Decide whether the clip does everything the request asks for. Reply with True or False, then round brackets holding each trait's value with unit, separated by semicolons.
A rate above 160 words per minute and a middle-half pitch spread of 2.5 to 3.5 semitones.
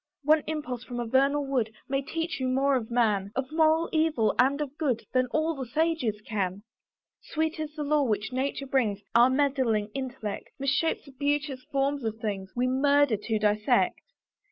False (180 wpm; 4.3 semitones)